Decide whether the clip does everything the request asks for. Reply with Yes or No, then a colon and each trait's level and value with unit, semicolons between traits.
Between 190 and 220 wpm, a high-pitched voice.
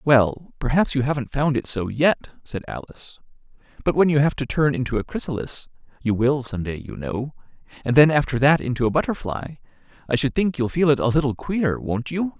No: average, 200 wpm; low, 135 Hz